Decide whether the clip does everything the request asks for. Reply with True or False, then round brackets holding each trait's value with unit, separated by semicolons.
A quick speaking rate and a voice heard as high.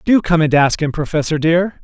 False (230 wpm; 165 Hz)